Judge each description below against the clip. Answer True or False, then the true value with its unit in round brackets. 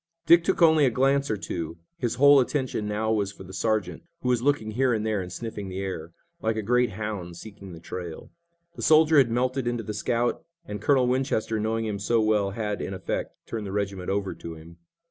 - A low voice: True (110 Hz)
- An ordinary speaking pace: False (220 wpm)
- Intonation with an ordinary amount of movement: True (4.2 semitones)